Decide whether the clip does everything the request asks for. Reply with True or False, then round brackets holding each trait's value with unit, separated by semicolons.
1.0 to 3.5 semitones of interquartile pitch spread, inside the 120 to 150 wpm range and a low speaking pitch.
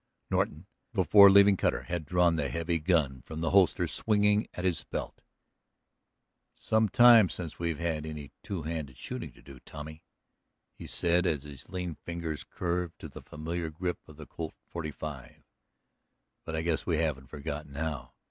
False (2.8 semitones; 165 wpm; 80 Hz)